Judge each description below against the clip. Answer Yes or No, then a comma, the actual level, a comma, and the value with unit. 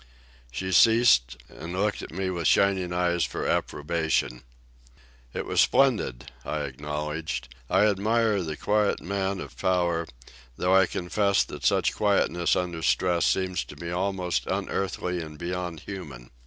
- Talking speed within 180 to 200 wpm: No, average, 140 wpm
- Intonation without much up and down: No, average, 3.2 semitones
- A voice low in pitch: Yes, very low, 90 Hz